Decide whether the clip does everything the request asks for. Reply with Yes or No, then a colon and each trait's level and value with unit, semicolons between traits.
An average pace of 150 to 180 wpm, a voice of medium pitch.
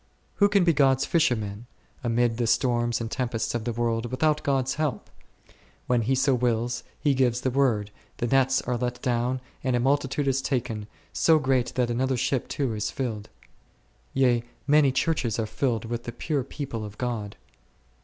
No: average, 175 wpm; low, 125 Hz